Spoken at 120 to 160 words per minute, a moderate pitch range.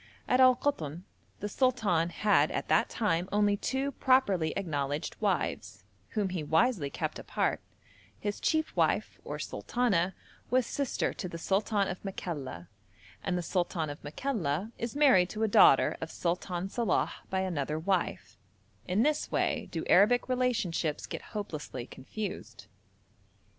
No: average, 140 wpm; wide, 6.2 semitones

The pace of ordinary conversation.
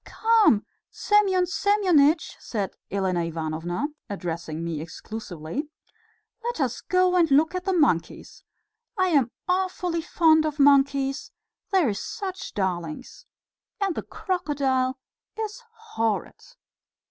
No: slow, 110 wpm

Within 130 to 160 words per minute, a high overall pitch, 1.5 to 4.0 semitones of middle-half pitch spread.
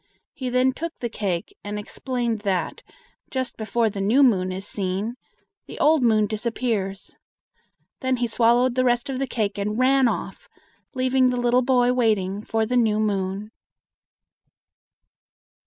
Yes: average, 150 wpm; high, 235 Hz; average, 3.5 semitones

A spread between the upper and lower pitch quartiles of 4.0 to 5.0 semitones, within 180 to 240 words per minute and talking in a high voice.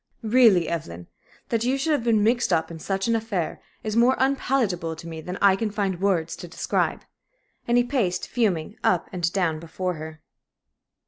No: wide, 5.6 semitones; average, 185 wpm; high, 195 Hz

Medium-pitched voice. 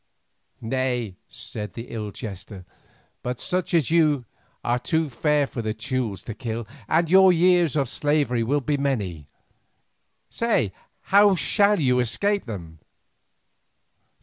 No: low, 130 Hz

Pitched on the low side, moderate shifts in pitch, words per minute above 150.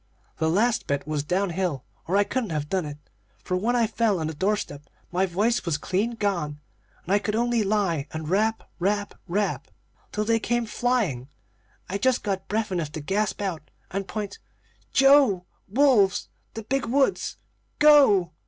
No: high, 200 Hz; average, 4.6 semitones; average, 170 wpm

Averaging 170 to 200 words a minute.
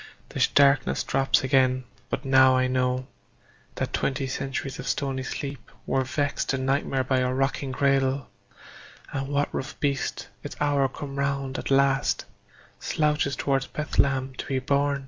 No: average, 150 wpm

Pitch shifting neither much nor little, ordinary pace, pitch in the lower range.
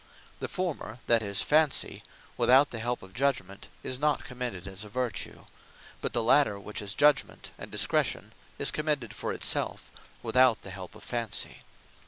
Yes: average, 5.0 semitones; average, 170 wpm; low, 120 Hz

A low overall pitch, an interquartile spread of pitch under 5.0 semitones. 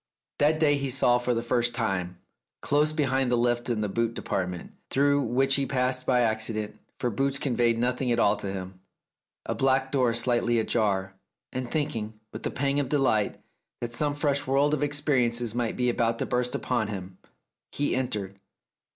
Yes: low, 120 Hz; average, 3.4 semitones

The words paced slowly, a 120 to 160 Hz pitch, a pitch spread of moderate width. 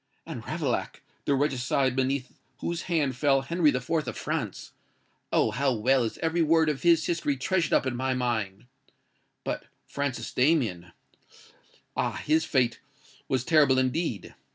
Yes: slow, 130 wpm; low, 135 Hz; average, 3.8 semitones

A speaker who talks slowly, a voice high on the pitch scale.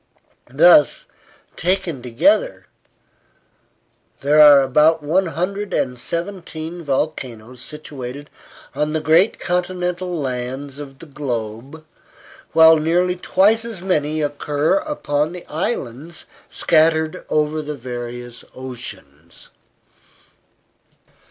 No: slow, 95 wpm; medium, 150 Hz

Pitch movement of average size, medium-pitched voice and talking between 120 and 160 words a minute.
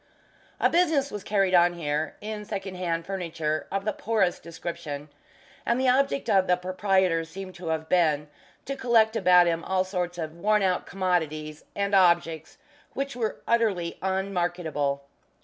Yes: average, 3.4 semitones; medium, 180 Hz; average, 155 wpm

